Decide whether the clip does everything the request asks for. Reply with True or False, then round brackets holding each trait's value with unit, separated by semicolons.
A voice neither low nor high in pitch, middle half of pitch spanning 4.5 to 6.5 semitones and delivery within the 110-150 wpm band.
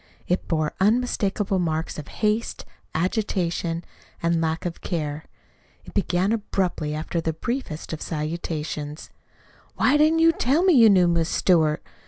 True (175 Hz; 4.9 semitones; 140 wpm)